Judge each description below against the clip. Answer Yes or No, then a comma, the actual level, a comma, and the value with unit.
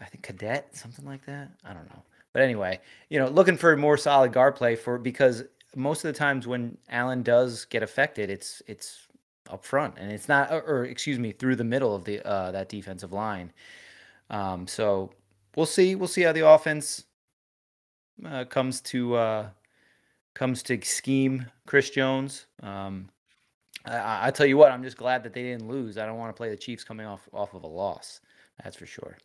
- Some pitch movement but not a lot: Yes, average, 4.5 semitones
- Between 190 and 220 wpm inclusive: Yes, average, 200 wpm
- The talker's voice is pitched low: Yes, low, 125 Hz